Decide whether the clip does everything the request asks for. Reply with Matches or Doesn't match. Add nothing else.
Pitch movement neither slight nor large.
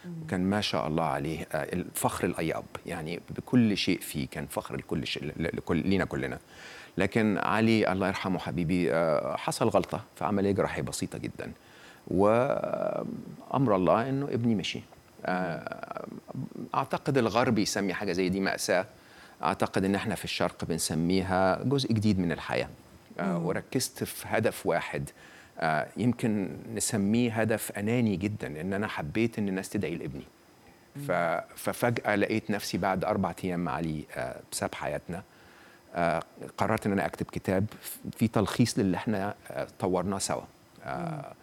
Matches